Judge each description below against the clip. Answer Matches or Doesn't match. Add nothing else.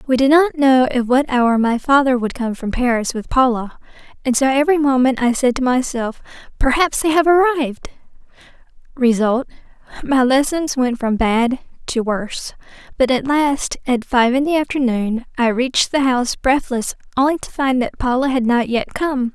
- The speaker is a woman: Matches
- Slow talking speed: Doesn't match